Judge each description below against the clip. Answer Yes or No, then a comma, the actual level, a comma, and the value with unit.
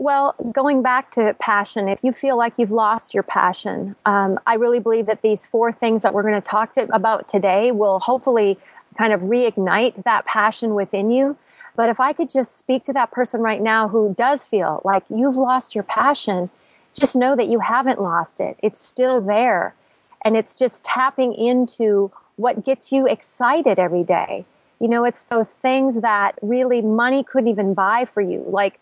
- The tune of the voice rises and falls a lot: No, average, 3.7 semitones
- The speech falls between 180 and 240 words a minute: Yes, average, 190 wpm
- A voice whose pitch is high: Yes, high, 230 Hz